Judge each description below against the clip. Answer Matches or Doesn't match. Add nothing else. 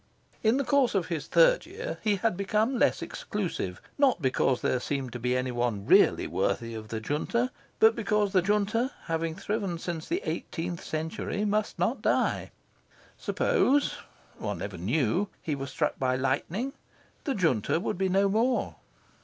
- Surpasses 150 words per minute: Matches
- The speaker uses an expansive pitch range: Matches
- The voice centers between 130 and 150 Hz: Doesn't match